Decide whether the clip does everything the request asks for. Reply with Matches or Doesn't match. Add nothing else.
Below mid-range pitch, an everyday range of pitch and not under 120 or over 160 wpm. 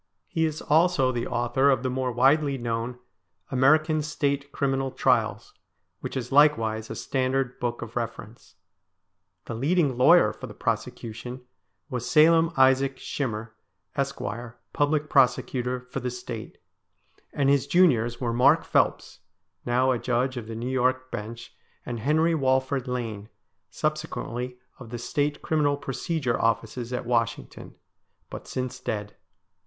Matches